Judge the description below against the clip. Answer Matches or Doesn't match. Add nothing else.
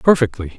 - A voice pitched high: Doesn't match